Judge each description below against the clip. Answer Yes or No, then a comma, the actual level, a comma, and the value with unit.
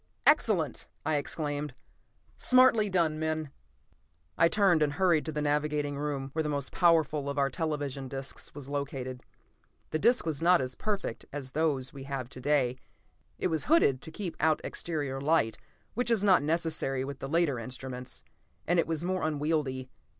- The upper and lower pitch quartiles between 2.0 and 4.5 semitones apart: Yes, average, 3.3 semitones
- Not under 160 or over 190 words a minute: Yes, average, 170 wpm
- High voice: No, medium, 150 Hz